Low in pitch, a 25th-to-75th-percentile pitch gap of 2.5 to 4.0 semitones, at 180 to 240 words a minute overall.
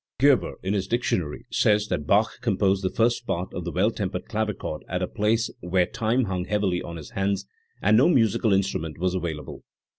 Yes: very low, 95 Hz; average, 3.3 semitones; average, 190 wpm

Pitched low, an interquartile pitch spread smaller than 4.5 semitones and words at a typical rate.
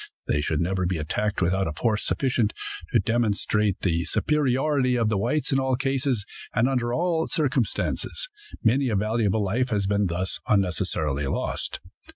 No: low, 110 Hz; wide, 5.4 semitones; average, 160 wpm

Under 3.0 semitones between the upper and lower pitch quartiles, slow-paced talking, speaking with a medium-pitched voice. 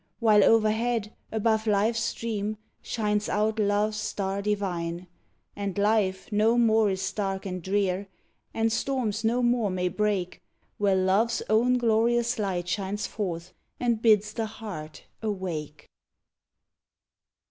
No: narrow, 2.6 semitones; slow, 125 wpm; high, 210 Hz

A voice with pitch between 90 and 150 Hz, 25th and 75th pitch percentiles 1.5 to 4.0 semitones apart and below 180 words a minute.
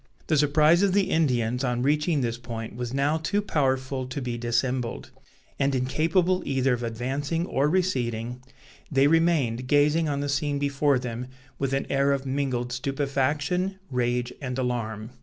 Yes: low, 135 Hz; average, 3.2 semitones; average, 160 wpm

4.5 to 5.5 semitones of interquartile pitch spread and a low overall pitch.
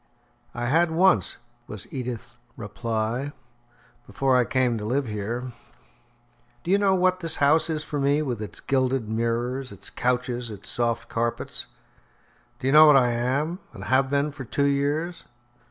No: average, 3.8 semitones; low, 130 Hz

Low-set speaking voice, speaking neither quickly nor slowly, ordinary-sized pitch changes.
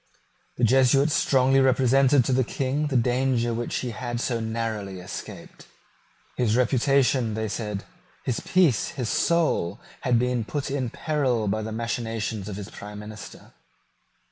Yes: low, 120 Hz; average, 145 wpm; average, 3.3 semitones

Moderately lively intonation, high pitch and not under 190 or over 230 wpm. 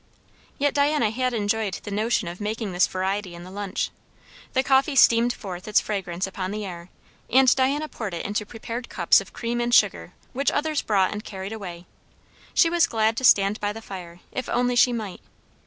Yes: average, 4.3 semitones; high, 215 Hz; average, 195 wpm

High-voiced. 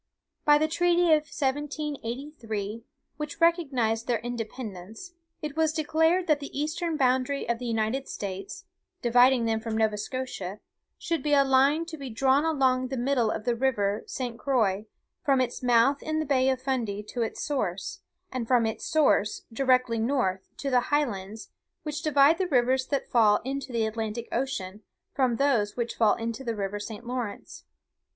Yes: very high, 255 Hz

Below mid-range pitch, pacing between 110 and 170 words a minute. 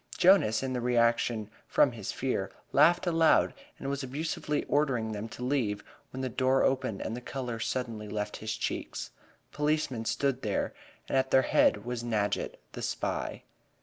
Yes: low, 125 Hz; average, 165 wpm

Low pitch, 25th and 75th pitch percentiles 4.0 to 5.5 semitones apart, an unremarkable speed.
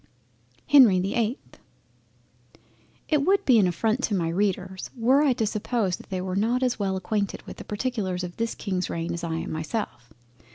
No: high, 205 Hz; average, 4.5 semitones; average, 190 wpm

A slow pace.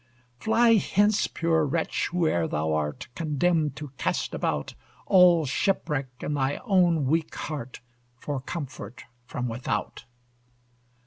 Yes: slow, 120 wpm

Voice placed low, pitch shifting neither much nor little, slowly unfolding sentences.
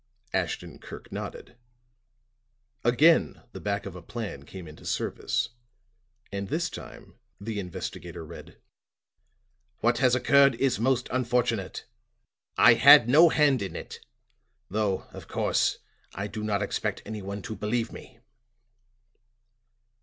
Yes: low, 110 Hz; average, 4.1 semitones; slow, 125 wpm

